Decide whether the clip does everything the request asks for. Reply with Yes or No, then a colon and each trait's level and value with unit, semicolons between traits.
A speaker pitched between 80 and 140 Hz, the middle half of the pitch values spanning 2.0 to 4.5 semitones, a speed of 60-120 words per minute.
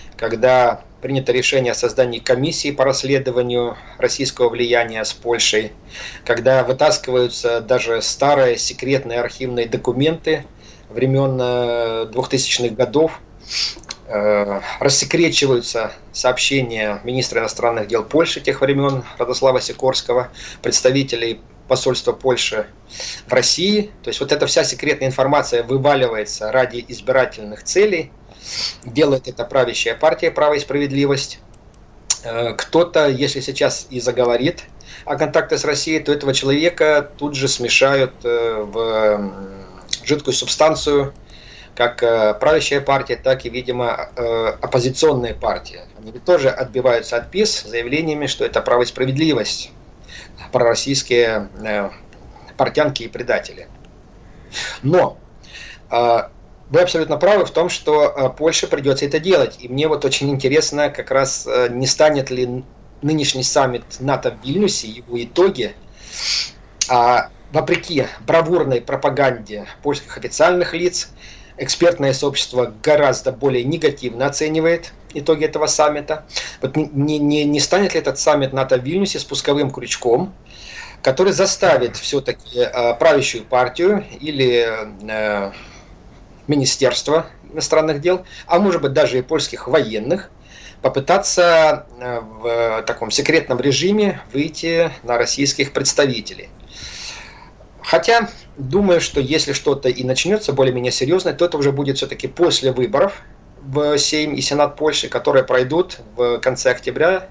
Yes: low, 135 Hz; average, 4.2 semitones; average, 115 wpm